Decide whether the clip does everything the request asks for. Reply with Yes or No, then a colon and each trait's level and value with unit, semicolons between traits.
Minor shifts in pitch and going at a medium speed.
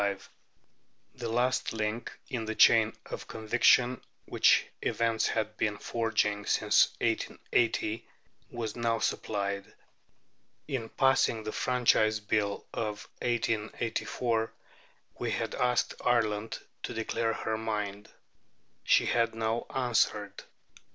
No: narrow, 1.7 semitones; slow, 105 wpm